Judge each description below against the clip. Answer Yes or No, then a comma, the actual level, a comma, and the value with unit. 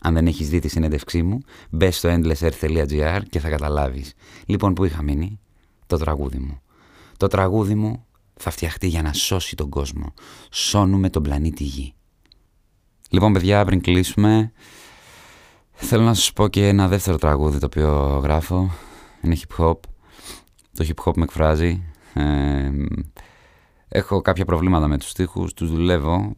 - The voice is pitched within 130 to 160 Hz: No, very low, 85 Hz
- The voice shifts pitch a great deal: No, average, 4.1 semitones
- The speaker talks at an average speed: Yes, average, 150 wpm